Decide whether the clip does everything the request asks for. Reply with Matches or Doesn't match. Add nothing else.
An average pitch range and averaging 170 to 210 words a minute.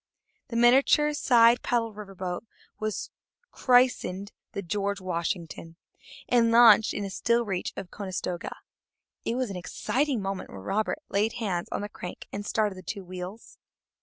Doesn't match